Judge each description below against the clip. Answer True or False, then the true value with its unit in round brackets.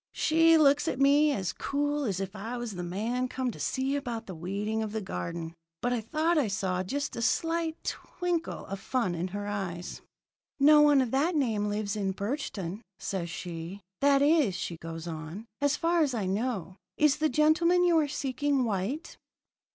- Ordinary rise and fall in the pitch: False (7.1 semitones)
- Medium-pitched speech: False (240 Hz)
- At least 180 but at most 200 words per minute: True (190 wpm)